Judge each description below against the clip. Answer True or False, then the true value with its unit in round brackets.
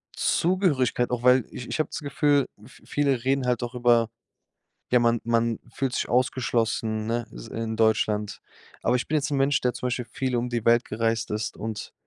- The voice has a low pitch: True (120 Hz)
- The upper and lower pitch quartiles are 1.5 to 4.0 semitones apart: True (2.4 semitones)